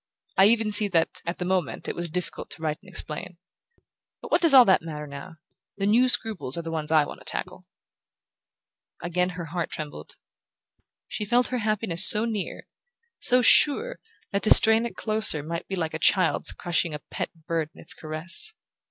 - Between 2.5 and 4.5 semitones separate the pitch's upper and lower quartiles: No, average, 5.1 semitones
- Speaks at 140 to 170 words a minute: No, average, 190 wpm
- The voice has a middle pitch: Yes, medium, 180 Hz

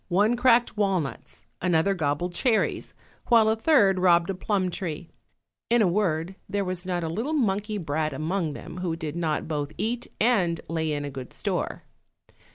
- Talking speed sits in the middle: Yes, average, 170 wpm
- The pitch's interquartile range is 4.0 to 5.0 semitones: Yes, average, 4.6 semitones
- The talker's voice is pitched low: No, medium, 180 Hz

